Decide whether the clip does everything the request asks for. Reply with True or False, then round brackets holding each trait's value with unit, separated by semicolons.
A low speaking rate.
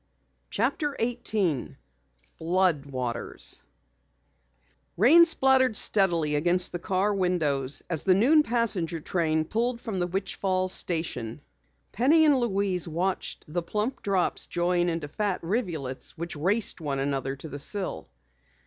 True (130 wpm)